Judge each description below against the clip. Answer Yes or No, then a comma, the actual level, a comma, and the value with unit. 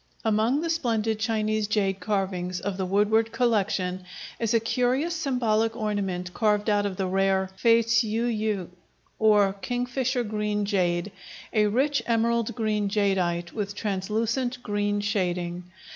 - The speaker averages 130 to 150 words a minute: Yes, slow, 135 wpm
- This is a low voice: No, high, 210 Hz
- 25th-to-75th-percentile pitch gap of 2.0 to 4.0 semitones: Yes, average, 2.9 semitones